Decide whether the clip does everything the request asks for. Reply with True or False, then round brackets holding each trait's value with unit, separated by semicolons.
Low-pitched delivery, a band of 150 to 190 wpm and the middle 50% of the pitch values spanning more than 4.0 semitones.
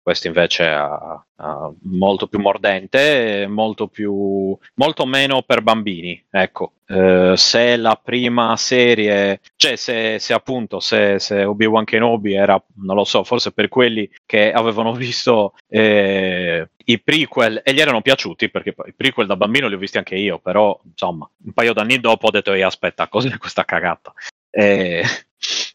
False (105 Hz; 155 wpm; 2.7 semitones)